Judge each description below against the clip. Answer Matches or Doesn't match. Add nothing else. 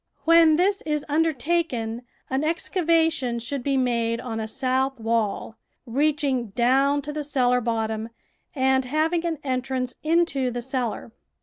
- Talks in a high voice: Matches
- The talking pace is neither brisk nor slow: Matches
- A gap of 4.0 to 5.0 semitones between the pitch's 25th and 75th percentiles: Matches